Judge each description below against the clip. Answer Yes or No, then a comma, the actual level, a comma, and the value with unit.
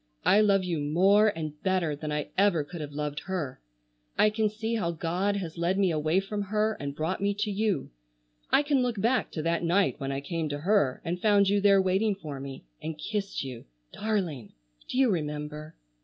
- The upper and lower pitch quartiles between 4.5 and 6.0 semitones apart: Yes, average, 5.2 semitones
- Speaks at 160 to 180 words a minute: No, average, 200 wpm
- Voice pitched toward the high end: No, medium, 180 Hz